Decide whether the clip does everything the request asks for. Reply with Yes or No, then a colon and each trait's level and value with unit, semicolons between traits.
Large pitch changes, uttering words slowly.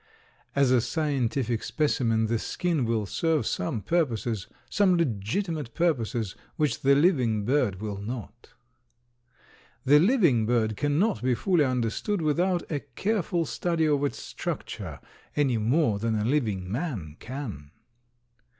Yes: wide, 6.1 semitones; slow, 130 wpm